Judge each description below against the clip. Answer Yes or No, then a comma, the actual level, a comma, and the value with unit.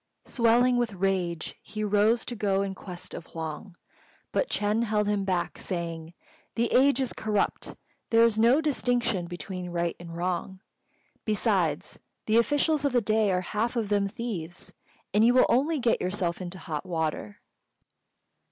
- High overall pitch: Yes, high, 205 Hz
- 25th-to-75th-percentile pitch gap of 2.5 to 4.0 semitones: No, average, 4.9 semitones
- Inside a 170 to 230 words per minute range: No, average, 160 wpm